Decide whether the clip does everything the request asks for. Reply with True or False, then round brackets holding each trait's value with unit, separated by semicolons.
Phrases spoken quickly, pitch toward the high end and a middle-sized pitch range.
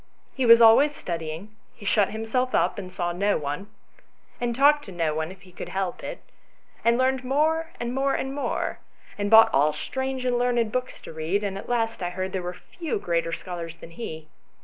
False (210 wpm; 210 Hz; 6.2 semitones)